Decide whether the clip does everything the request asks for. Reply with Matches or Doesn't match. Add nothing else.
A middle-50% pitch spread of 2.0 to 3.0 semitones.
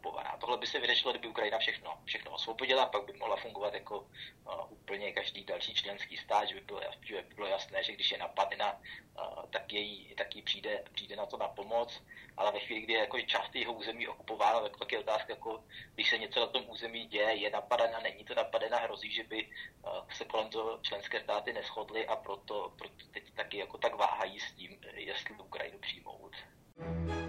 Matches